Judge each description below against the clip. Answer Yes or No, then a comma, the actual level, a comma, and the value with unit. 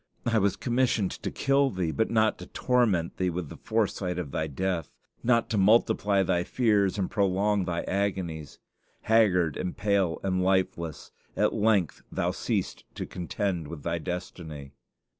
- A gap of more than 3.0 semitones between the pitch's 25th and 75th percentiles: Yes, average, 3.6 semitones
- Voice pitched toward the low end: Yes, very low, 95 Hz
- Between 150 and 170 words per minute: Yes, average, 160 wpm